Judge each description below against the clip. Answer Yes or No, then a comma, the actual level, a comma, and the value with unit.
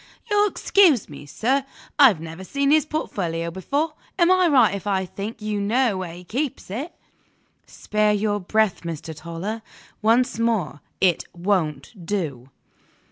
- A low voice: No, high, 210 Hz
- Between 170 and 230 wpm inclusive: No, average, 145 wpm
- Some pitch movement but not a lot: No, wide, 7.2 semitones